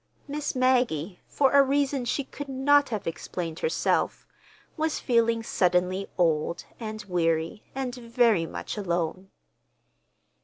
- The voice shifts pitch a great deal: Yes, wide, 7.0 semitones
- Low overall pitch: No, high, 230 Hz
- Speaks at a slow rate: Yes, slow, 120 wpm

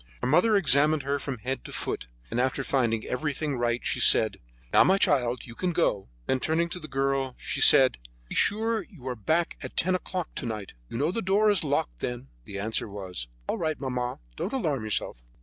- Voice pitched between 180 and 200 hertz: No, low, 135 Hz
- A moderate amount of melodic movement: No, wide, 5.9 semitones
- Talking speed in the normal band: No, fast, 210 wpm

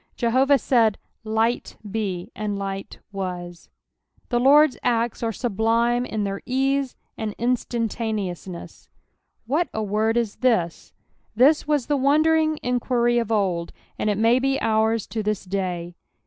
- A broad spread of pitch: No, average, 3.7 semitones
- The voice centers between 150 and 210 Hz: No, high, 225 Hz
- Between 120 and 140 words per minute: Yes, slow, 135 wpm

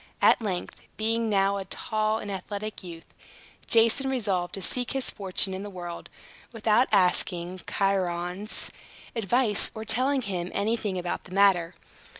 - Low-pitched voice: No, high, 200 Hz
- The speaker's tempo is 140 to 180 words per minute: Yes, average, 145 wpm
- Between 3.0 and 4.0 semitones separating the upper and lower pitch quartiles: Yes, average, 3.3 semitones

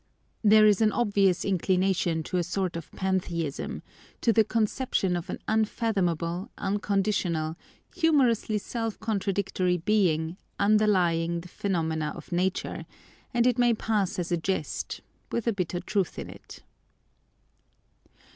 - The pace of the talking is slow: Yes, slow, 125 wpm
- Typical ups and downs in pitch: Yes, average, 3.7 semitones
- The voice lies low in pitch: No, high, 195 Hz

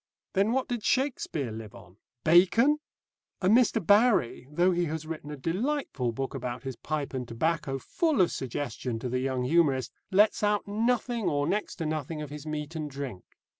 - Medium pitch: Yes, medium, 155 Hz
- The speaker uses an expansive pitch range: Yes, wide, 7.6 semitones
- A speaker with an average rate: Yes, average, 180 wpm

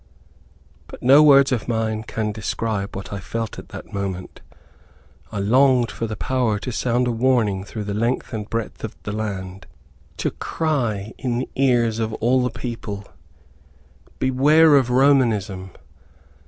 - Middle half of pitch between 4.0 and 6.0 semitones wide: No, average, 3.6 semitones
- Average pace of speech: Yes, average, 155 wpm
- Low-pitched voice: Yes, low, 115 Hz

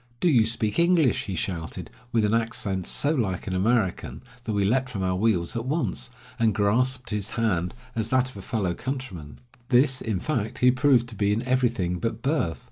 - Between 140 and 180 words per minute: No, average, 200 wpm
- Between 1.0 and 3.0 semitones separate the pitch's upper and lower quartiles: No, average, 4.7 semitones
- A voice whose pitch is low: Yes, low, 115 Hz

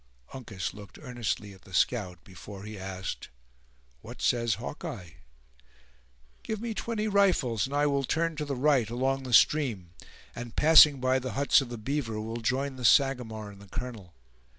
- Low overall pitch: Yes, low, 125 Hz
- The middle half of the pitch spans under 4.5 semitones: No, average, 5.1 semitones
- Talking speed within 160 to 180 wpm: Yes, average, 170 wpm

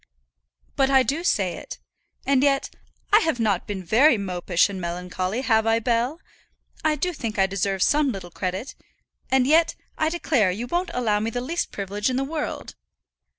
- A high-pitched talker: Yes, high, 230 Hz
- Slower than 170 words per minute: No, average, 180 wpm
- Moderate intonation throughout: No, wide, 6.2 semitones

